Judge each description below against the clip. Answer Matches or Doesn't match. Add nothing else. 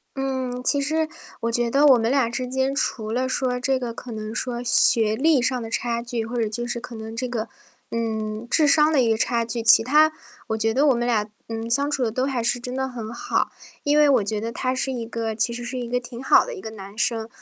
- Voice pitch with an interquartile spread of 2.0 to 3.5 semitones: Matches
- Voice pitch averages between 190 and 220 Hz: Doesn't match